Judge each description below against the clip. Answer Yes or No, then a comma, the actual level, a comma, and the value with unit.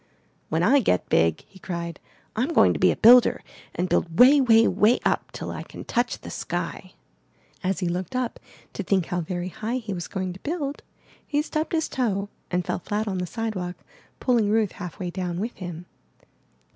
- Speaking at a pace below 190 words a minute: No, average, 195 wpm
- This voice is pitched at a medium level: No, high, 200 Hz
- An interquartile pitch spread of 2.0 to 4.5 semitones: No, average, 5.3 semitones